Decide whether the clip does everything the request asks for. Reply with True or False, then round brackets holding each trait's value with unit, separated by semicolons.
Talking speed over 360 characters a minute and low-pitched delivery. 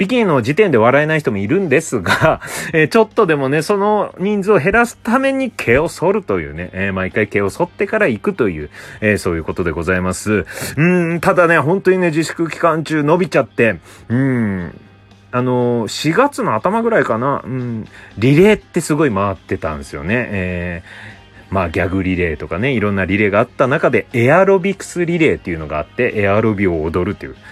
True (400 characters per minute; 125 Hz)